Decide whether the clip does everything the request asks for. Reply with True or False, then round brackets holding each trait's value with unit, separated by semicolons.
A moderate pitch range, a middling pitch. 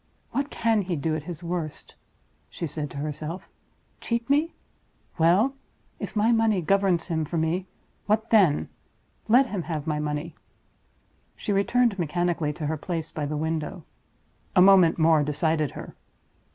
True (4.5 semitones; 170 Hz)